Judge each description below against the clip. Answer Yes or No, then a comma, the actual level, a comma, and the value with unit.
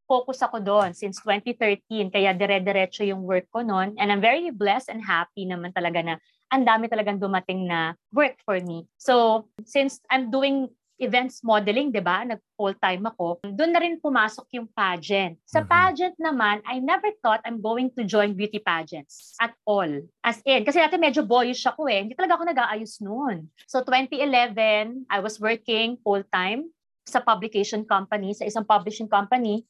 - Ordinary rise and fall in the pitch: Yes, average, 4.1 semitones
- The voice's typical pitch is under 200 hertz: No, high, 220 Hz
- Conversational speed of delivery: No, fast, 170 wpm